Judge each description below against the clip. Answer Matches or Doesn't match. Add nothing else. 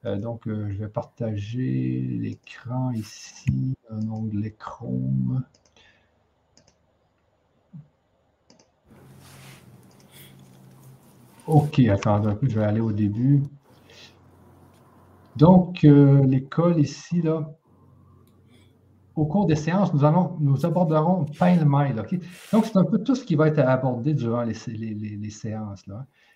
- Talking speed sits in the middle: Doesn't match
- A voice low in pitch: Matches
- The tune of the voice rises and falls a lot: Matches